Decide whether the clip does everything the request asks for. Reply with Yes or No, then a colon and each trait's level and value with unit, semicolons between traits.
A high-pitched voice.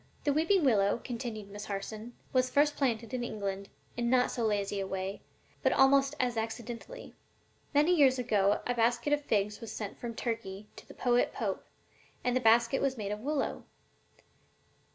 Yes: high, 235 Hz